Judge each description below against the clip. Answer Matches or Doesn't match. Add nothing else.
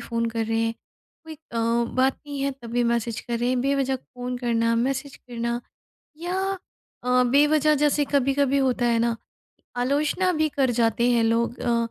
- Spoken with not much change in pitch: Doesn't match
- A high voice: Matches